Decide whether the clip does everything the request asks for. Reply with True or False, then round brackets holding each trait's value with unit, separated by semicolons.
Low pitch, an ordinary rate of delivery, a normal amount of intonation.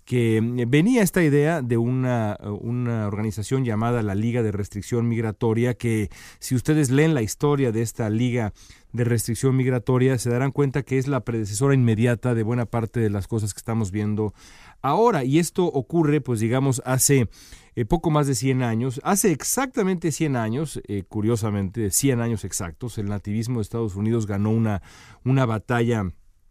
True (120 Hz; 170 wpm; 3.5 semitones)